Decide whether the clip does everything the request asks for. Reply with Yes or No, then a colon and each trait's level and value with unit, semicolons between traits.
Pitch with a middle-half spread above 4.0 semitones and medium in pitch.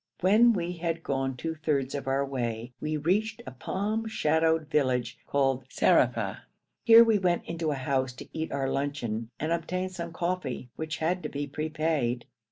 Yes: average, 4.4 semitones; medium, 155 Hz